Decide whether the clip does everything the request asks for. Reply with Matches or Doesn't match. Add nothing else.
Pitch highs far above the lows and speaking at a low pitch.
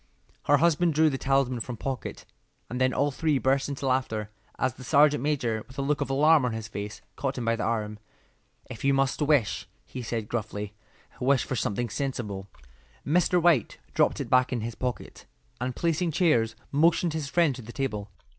Doesn't match